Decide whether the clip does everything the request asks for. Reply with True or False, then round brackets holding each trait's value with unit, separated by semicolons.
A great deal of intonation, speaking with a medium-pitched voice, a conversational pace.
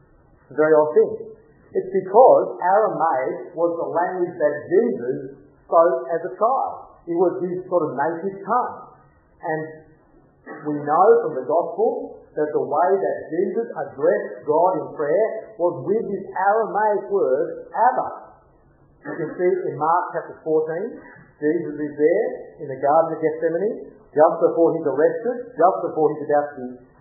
True (7.7 semitones; 170 Hz; 155 wpm)